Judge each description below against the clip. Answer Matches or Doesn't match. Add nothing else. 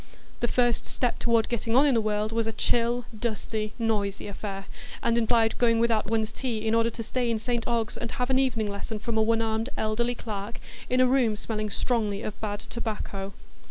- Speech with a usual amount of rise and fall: Doesn't match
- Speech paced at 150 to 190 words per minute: Doesn't match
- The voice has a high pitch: Matches